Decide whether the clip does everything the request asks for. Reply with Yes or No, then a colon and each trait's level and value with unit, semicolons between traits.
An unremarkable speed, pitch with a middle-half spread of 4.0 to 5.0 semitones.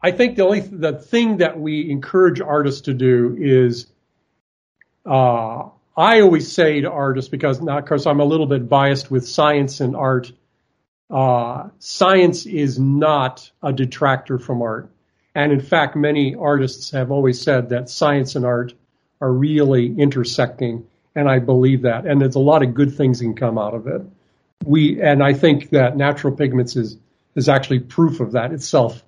No: average, 175 wpm; average, 2.8 semitones